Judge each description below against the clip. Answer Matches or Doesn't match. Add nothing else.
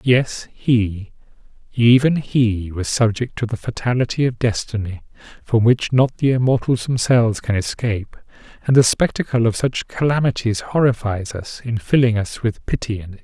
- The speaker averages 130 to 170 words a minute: Matches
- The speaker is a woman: Doesn't match